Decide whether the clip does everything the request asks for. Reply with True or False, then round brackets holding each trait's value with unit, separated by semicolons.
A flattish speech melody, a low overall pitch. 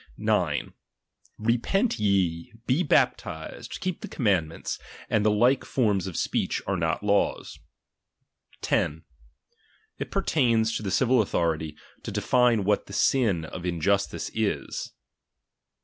False (5.2 semitones; 105 Hz)